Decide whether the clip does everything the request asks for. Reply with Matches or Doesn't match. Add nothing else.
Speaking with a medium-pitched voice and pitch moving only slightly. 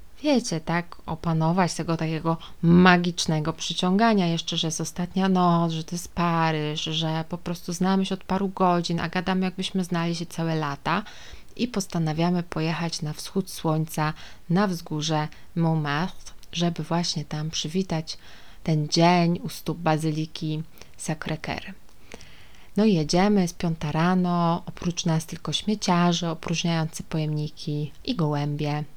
Matches